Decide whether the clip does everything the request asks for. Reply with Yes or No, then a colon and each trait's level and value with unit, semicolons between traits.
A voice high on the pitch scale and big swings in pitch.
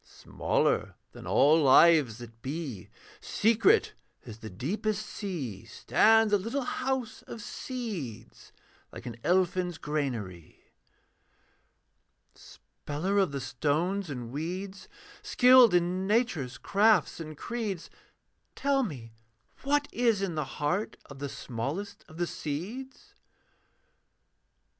No: medium, 175 Hz; wide, 7.5 semitones